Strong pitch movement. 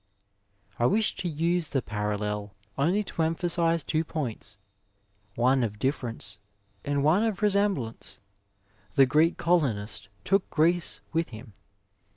Yes: wide, 7.9 semitones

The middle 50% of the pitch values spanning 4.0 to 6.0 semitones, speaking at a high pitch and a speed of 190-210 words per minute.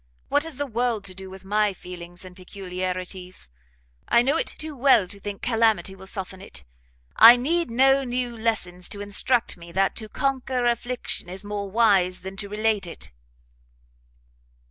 No: average, 4.6 semitones; high, 205 Hz; average, 165 wpm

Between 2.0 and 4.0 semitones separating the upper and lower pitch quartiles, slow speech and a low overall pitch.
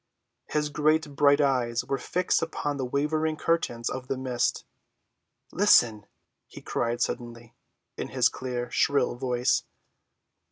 Yes: average, 3.6 semitones; slow, 125 wpm; low, 130 Hz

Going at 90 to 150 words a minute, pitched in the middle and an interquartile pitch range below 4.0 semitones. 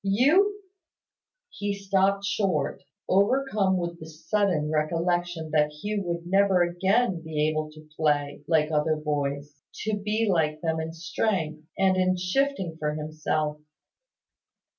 No: slow, 135 wpm; medium, 175 Hz; average, 4.4 semitones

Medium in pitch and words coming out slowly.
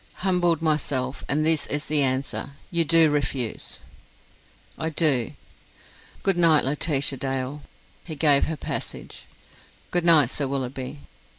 Yes: medium, 150 Hz; slow, 125 wpm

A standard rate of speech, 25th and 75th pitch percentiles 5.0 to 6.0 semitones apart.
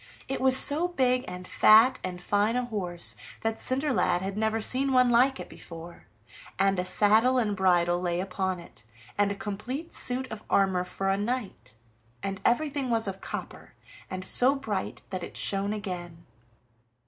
Yes: average, 170 wpm; average, 5.3 semitones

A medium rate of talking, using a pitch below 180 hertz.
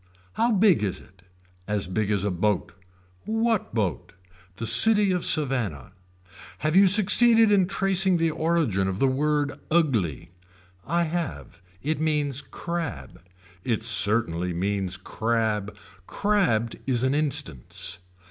No: slow, 130 wpm; low, 135 Hz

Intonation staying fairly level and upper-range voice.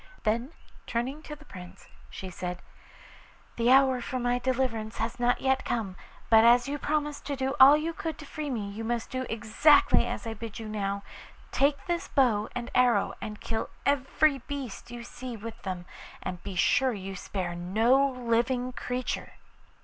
No: average, 3.7 semitones; high, 245 Hz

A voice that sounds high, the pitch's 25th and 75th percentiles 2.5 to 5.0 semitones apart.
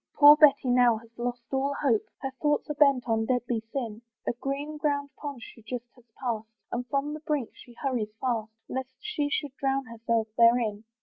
Yes: very high, 250 Hz; average, 3.5 semitones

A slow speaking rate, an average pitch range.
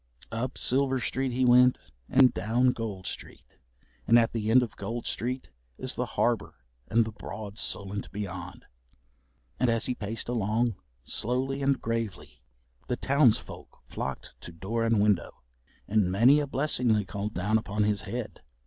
No: average, 155 wpm; average, 3.4 semitones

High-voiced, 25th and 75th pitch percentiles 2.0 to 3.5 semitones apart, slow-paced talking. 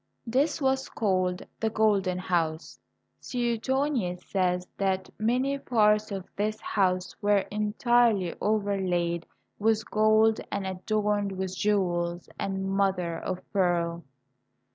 Yes: high, 200 Hz; average, 3.1 semitones; slow, 110 wpm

